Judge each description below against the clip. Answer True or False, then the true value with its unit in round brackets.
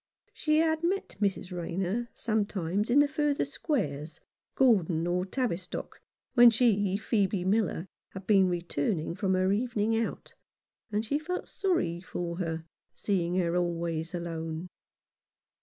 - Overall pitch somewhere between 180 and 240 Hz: True (190 Hz)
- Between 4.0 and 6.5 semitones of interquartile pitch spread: True (5.5 semitones)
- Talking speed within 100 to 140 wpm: True (135 wpm)